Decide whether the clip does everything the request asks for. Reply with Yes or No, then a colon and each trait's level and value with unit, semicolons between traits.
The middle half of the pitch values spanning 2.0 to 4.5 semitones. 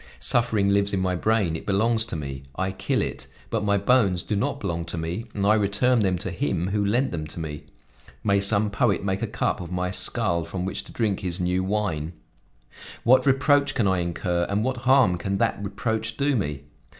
Yes: average, 3.8 semitones